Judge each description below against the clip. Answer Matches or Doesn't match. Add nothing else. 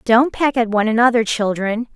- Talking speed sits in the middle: Matches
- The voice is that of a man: Doesn't match